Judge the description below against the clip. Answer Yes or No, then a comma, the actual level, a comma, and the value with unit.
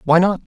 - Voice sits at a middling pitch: Yes, medium, 180 Hz